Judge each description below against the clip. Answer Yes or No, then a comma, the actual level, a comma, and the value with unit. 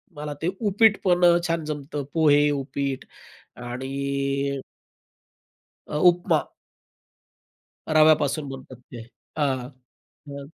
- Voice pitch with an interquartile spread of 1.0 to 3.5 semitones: Yes, narrow, 2.6 semitones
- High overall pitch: No, medium, 145 Hz